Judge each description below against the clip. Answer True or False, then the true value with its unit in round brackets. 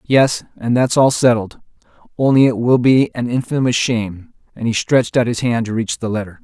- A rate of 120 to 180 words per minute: False (205 wpm)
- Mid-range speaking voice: False (120 Hz)